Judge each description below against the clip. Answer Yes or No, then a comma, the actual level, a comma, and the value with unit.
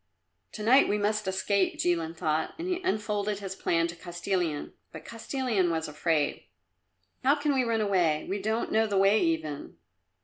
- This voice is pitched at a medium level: No, high, 195 Hz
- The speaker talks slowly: No, average, 170 wpm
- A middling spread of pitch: Yes, average, 4.8 semitones